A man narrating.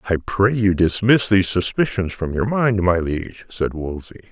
Yes: male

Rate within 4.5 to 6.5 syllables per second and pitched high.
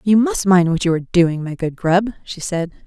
No: 5.1 syllables/s; medium, 180 Hz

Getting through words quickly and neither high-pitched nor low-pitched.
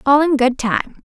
No: fast, 225 wpm; very high, 275 Hz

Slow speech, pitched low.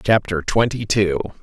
Yes: slow, 125 wpm; low, 100 Hz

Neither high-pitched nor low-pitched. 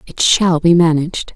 Yes: medium, 165 Hz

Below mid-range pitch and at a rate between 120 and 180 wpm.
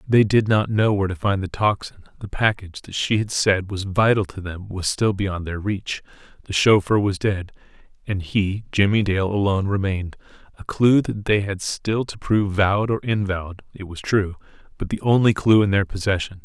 No: low, 100 Hz; average, 195 wpm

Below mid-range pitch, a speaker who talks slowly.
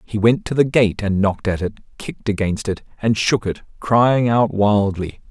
No: low, 105 Hz; fast, 205 wpm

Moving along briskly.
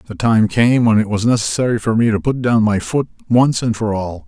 Yes: fast, 255 wpm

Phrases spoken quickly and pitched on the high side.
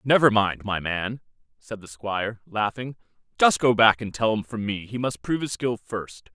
No: fast, 210 wpm; low, 110 Hz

